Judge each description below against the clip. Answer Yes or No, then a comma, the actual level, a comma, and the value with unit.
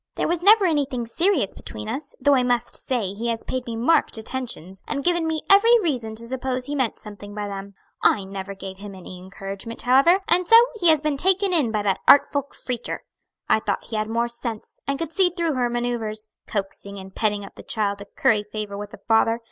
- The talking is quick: Yes, fast, 220 wpm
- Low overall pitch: No, high, 235 Hz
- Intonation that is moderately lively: No, wide, 5.9 semitones